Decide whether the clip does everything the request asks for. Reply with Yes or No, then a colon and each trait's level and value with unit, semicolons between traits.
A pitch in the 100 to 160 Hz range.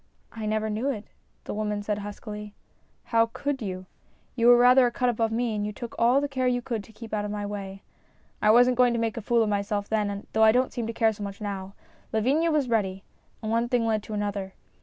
No: high, 220 Hz